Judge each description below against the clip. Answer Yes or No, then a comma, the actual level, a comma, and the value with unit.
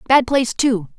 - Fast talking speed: No, average, 185 wpm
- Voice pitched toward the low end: No, high, 245 Hz